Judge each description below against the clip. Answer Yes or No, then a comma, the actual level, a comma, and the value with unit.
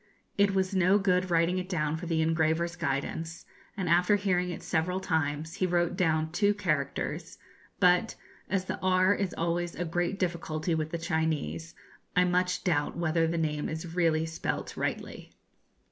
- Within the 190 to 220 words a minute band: No, average, 165 wpm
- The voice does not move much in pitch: Yes, narrow, 2.2 semitones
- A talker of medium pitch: Yes, medium, 170 Hz